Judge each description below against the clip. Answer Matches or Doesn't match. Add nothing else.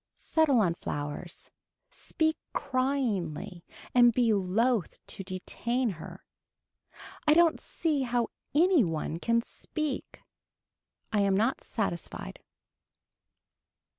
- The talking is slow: Matches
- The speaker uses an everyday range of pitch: Doesn't match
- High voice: Matches